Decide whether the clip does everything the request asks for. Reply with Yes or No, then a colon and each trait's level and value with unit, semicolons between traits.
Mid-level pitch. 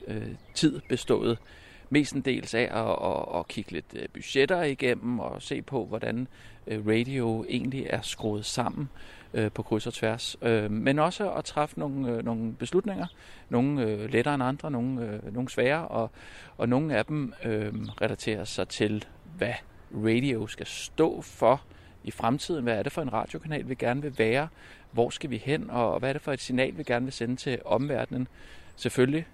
No: low, 120 Hz